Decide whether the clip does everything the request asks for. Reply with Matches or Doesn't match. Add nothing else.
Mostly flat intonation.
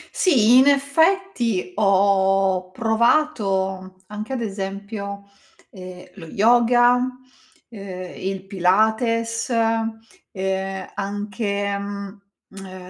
Doesn't match